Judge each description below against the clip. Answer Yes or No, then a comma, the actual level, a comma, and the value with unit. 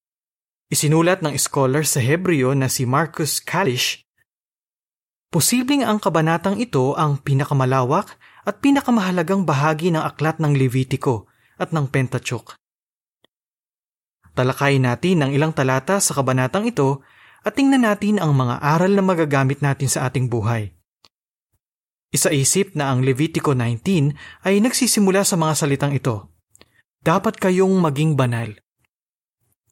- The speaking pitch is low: No, medium, 150 Hz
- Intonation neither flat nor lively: No, wide, 5.9 semitones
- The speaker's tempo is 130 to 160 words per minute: No, average, 120 wpm